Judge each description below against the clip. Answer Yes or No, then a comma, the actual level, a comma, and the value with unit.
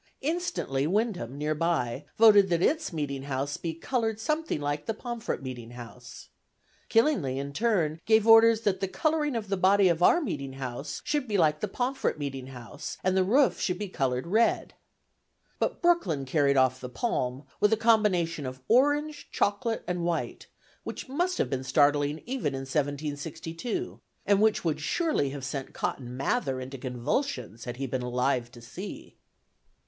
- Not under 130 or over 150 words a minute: No, average, 170 wpm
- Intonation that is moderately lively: No, wide, 8.8 semitones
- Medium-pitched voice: Yes, medium, 165 Hz